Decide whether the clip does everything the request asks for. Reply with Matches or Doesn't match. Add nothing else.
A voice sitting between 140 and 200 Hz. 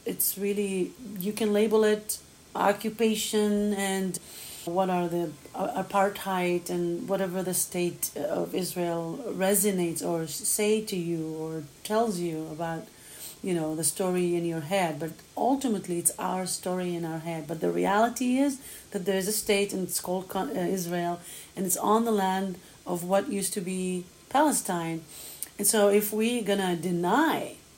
Matches